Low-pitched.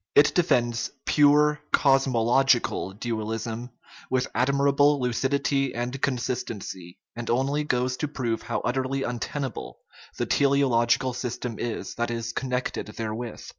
Yes: low, 125 Hz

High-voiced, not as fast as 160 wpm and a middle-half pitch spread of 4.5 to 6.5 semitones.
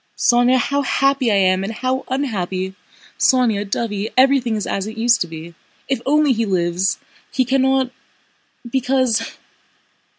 Yes: high, 235 Hz; average, 140 wpm; average, 4.8 semitones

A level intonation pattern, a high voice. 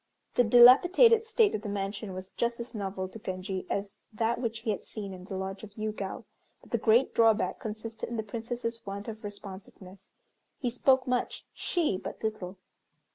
No: average, 3.1 semitones; high, 215 Hz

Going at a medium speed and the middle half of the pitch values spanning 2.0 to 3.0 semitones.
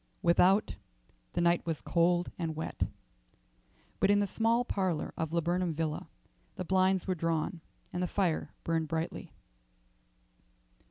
No: slow, 130 wpm; narrow, 2.4 semitones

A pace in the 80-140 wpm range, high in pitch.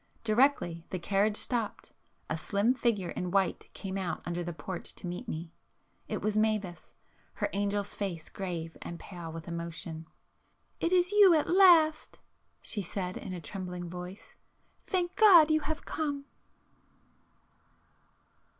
Yes: slow, 135 wpm; high, 195 Hz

